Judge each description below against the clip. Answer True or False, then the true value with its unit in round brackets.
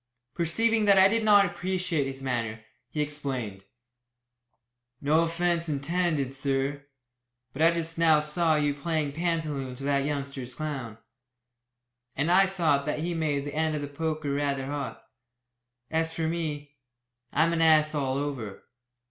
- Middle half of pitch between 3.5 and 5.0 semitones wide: False (3.0 semitones)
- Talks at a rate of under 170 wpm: True (150 wpm)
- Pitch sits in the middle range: True (150 Hz)